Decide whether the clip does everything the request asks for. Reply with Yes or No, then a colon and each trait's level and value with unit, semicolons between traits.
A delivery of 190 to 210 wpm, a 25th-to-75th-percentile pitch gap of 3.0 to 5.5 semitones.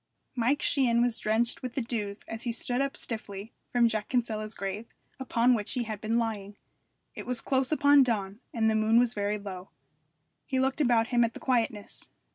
No: average, 195 wpm; narrow, 2.5 semitones